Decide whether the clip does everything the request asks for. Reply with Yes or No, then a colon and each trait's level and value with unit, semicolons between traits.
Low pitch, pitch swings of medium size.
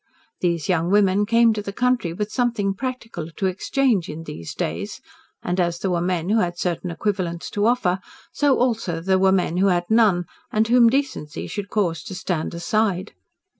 No: high, 190 Hz; average, 4.2 semitones